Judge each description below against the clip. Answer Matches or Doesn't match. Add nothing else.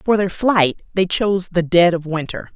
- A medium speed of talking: Doesn't match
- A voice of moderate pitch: Matches